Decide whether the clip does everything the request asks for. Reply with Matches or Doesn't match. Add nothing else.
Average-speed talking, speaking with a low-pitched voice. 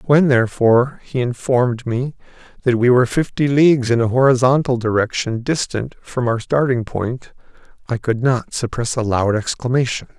Matches